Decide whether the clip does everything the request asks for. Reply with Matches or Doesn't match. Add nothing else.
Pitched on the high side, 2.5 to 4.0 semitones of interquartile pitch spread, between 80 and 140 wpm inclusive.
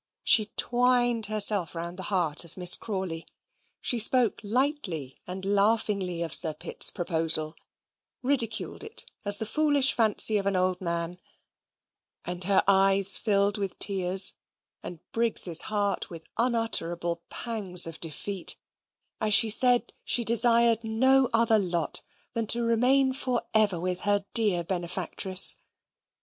Doesn't match